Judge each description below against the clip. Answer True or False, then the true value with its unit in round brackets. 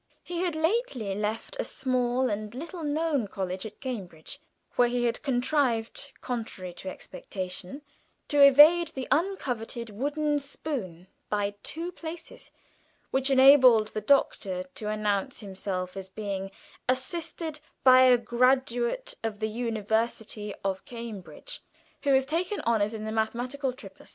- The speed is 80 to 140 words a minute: True (135 wpm)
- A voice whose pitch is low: False (240 Hz)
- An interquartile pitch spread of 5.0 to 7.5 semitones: True (5.3 semitones)